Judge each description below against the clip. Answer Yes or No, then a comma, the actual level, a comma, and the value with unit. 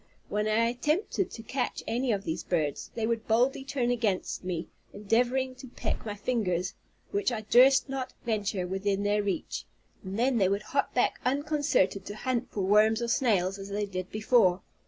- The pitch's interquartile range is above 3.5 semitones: Yes, average, 4.2 semitones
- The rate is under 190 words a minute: Yes, average, 180 wpm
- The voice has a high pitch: Yes, high, 220 Hz